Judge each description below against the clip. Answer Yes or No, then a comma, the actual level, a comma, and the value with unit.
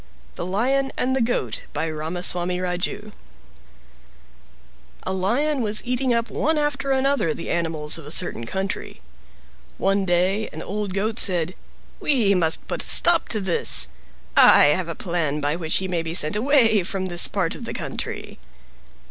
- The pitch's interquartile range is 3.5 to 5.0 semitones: No, wide, 5.4 semitones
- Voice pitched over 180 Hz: Yes, high, 190 Hz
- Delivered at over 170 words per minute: No, average, 165 wpm